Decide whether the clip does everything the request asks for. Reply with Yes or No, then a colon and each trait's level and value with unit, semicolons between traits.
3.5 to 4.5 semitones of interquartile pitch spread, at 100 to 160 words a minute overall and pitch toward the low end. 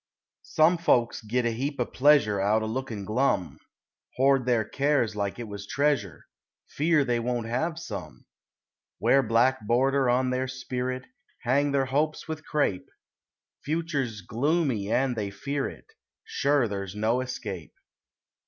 Yes: average, 4.2 semitones; average, 145 wpm; low, 125 Hz